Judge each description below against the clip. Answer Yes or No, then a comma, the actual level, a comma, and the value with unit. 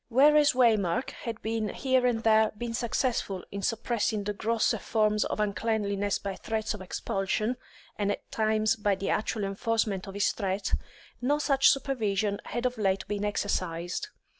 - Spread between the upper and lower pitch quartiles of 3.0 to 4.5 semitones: No, narrow, 2.5 semitones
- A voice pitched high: Yes, high, 215 Hz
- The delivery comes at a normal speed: Yes, average, 155 wpm